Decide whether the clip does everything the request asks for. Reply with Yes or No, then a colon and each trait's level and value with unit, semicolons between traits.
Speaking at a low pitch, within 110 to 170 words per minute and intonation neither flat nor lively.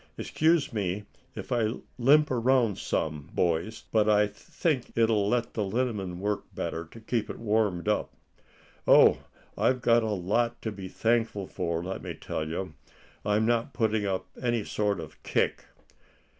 Yes: low, 110 Hz; average, 155 wpm; average, 3.6 semitones